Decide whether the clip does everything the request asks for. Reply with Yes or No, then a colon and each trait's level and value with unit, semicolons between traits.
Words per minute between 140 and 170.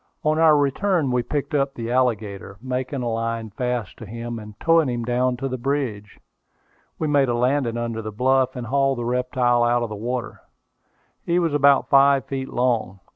No: average, 190 wpm